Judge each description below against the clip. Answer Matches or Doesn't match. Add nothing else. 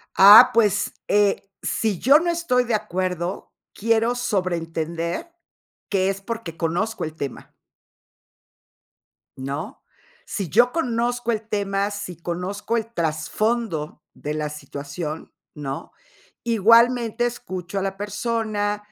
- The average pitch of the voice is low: Doesn't match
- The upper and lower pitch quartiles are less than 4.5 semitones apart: Doesn't match